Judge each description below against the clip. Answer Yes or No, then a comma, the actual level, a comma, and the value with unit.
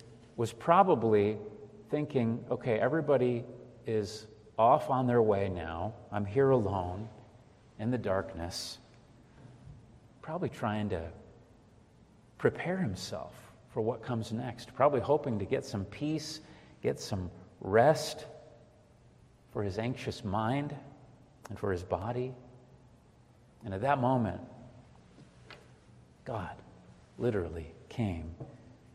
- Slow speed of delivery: Yes, slow, 105 wpm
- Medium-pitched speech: No, low, 115 Hz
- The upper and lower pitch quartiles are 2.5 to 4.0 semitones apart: Yes, average, 3.2 semitones